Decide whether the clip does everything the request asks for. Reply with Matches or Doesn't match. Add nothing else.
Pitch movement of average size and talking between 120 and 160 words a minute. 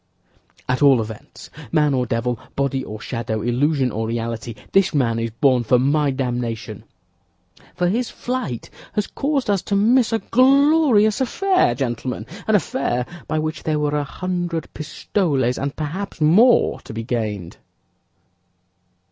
Doesn't match